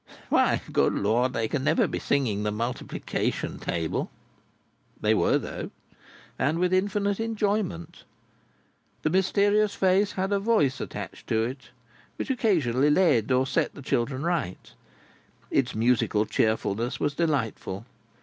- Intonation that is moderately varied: No, wide, 8.6 semitones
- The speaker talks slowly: Yes, slow, 130 wpm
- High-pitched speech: No, medium, 140 Hz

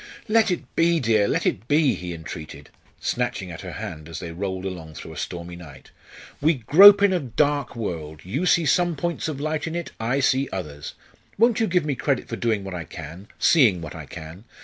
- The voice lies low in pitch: Yes, low, 115 Hz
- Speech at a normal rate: No, fast, 215 wpm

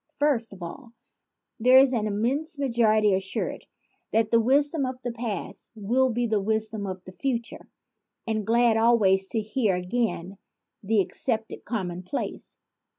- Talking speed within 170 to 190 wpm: No, average, 150 wpm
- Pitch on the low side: No, high, 225 Hz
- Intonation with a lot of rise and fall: No, average, 3.3 semitones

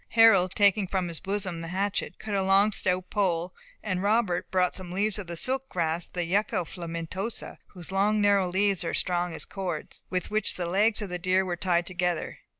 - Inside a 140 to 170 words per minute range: No, average, 200 wpm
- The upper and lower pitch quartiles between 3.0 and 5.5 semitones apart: No, narrow, 2.5 semitones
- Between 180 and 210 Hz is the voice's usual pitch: Yes, medium, 185 Hz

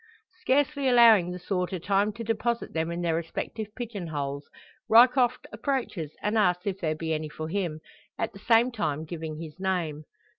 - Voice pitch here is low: No, medium, 185 Hz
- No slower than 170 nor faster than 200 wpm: Yes, average, 175 wpm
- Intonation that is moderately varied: No, wide, 6.1 semitones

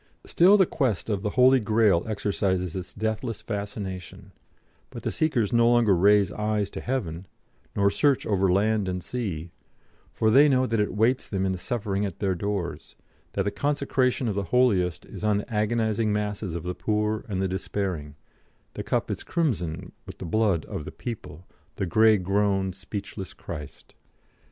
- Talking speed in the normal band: Yes, average, 175 wpm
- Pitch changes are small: No, average, 3.3 semitones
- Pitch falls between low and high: No, low, 105 Hz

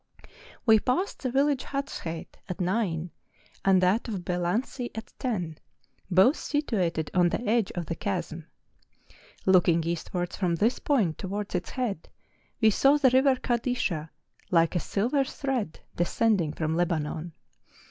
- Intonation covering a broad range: Yes, wide, 6.3 semitones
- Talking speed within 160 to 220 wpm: No, average, 140 wpm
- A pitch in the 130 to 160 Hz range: No, high, 190 Hz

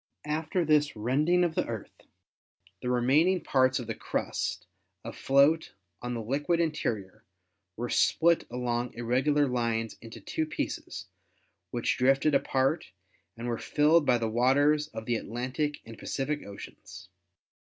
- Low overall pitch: Yes, low, 130 Hz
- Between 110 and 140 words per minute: Yes, slow, 135 wpm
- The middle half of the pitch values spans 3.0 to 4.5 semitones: Yes, average, 4.1 semitones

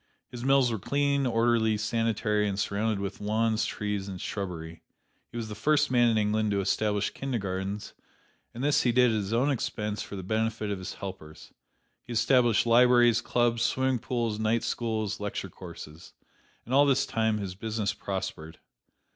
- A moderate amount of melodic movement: Yes, average, 3.0 semitones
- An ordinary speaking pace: Yes, average, 170 wpm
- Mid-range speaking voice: No, low, 110 Hz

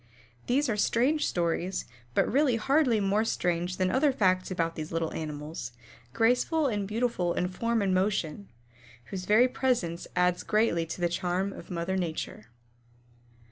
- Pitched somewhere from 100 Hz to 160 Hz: No, high, 190 Hz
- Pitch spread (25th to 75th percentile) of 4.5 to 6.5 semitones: Yes, average, 5.1 semitones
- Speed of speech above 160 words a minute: No, average, 150 wpm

